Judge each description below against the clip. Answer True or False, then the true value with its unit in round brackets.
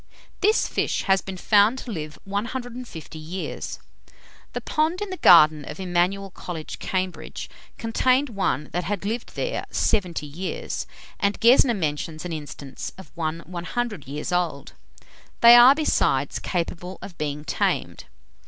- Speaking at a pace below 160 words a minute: True (140 wpm)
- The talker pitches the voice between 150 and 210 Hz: True (185 Hz)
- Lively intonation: True (6.6 semitones)